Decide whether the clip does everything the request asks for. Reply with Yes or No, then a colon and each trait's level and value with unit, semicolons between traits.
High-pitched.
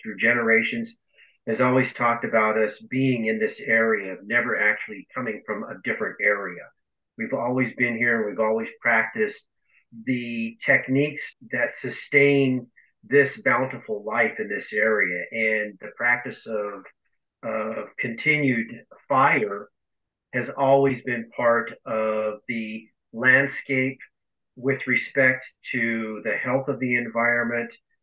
No: low, 120 Hz